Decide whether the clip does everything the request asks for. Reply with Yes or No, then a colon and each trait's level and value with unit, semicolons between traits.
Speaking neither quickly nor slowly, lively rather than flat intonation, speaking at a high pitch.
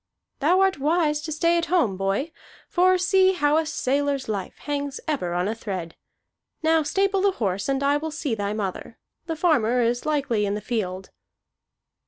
Yes: average, 180 wpm; wide, 7.4 semitones; very high, 285 Hz